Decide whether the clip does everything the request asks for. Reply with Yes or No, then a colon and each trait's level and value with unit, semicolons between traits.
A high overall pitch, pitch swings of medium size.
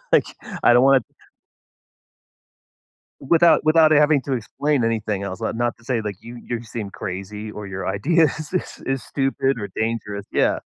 No: low, 120 Hz; average, 4.8 semitones